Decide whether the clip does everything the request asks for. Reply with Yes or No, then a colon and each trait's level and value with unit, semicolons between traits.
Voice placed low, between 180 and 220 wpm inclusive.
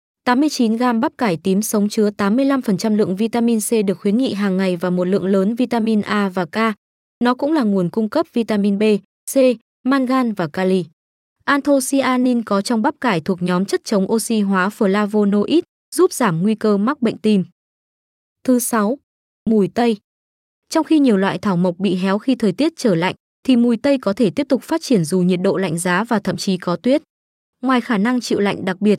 No: high, 215 Hz; average, 200 wpm